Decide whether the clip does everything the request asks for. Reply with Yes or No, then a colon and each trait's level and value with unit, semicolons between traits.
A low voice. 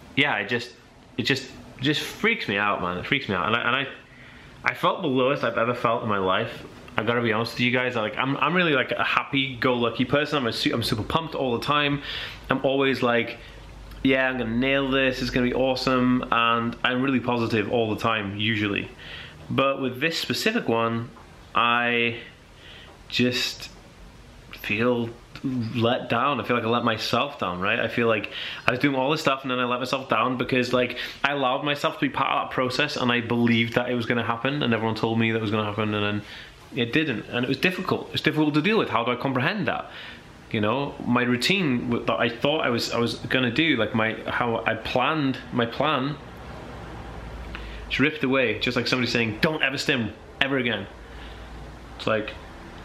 Yes: low, 120 Hz